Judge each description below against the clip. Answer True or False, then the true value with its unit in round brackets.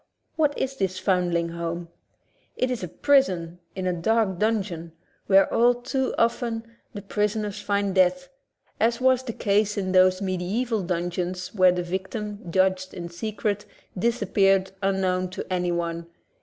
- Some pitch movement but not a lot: True (3.5 semitones)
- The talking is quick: False (140 wpm)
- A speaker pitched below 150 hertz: False (190 Hz)